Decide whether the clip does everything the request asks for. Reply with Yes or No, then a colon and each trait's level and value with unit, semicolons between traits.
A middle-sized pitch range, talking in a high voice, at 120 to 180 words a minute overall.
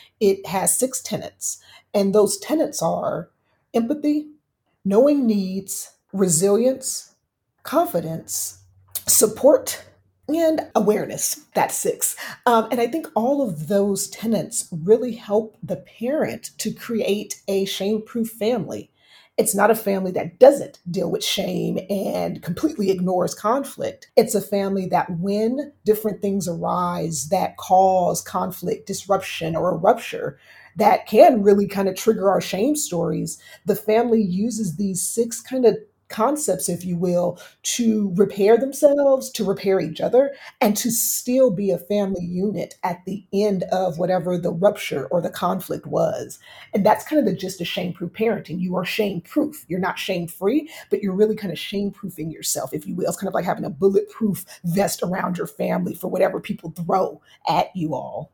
Yes: average, 3.9 semitones; high, 200 Hz; average, 160 wpm